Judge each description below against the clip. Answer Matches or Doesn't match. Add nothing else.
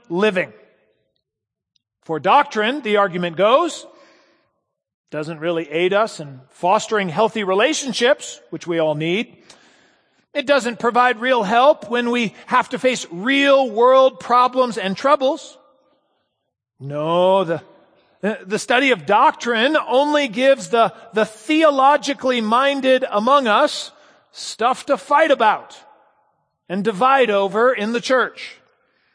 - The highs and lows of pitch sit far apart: Matches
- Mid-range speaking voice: Doesn't match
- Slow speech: Matches